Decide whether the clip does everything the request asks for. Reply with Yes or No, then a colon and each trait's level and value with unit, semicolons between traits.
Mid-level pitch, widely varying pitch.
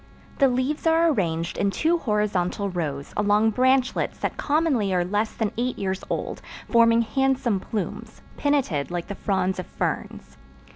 No: high, 210 Hz; wide, 5.8 semitones